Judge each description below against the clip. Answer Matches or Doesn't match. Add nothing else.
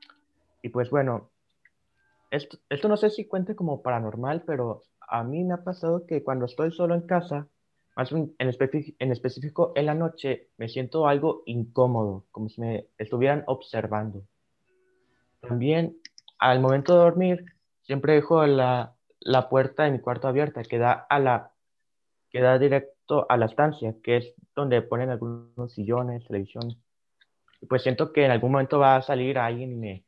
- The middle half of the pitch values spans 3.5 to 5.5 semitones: Matches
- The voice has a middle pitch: Doesn't match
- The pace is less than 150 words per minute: Doesn't match